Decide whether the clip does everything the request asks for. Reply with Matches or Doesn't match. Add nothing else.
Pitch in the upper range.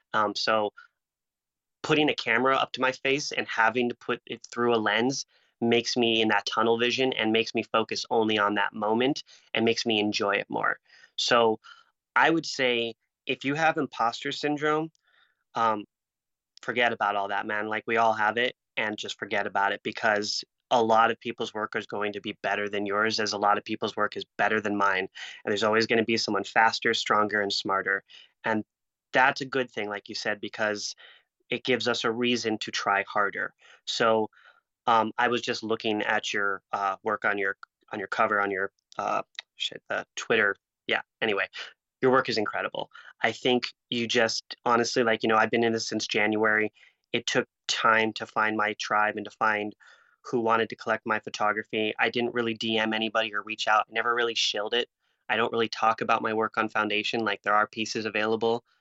Doesn't match